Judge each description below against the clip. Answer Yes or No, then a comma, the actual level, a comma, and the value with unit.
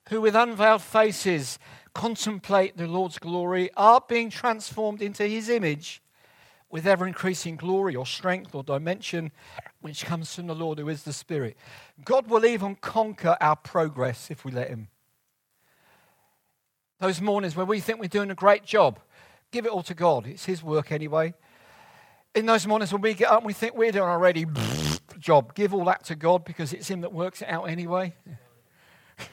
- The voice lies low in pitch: No, medium, 180 Hz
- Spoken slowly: No, average, 180 wpm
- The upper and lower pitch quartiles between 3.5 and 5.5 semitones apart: Yes, average, 5.0 semitones